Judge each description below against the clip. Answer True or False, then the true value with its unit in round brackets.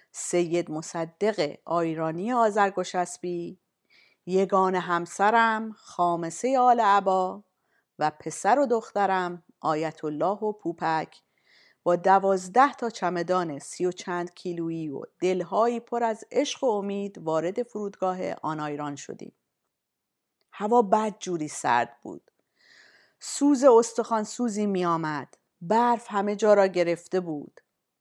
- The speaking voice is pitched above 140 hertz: True (185 Hz)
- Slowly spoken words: False (115 wpm)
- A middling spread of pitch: True (4.1 semitones)